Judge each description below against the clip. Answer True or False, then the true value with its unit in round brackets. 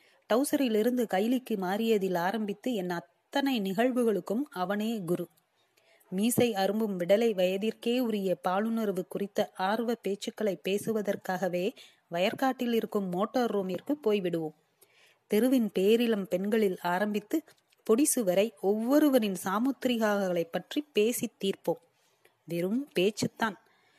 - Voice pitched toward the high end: True (210 Hz)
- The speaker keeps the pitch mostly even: False (4.1 semitones)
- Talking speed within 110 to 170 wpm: False (90 wpm)